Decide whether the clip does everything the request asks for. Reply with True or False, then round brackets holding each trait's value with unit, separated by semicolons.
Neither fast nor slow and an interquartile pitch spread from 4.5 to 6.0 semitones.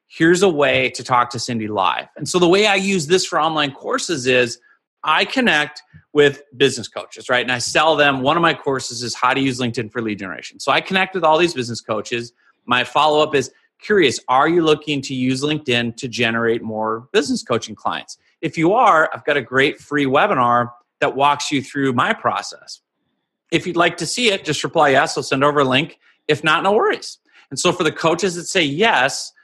False (220 wpm; 4.9 semitones)